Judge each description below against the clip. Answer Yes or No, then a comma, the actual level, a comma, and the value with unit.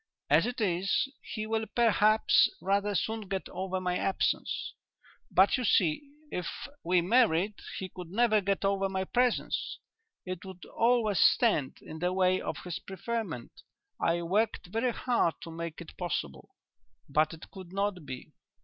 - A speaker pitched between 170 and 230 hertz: Yes, high, 190 Hz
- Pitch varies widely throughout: No, average, 3.7 semitones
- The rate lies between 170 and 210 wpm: No, average, 155 wpm